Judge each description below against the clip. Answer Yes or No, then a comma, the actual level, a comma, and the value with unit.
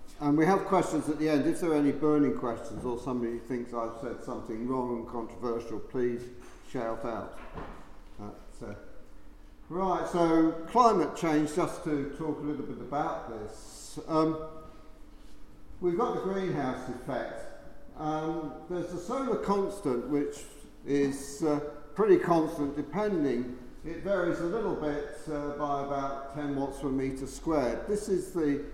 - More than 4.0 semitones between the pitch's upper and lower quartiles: Yes, average, 4.5 semitones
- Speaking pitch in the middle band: Yes, medium, 145 Hz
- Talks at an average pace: Yes, average, 150 wpm